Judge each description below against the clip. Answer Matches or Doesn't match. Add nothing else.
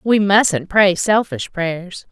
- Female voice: Matches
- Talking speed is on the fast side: Doesn't match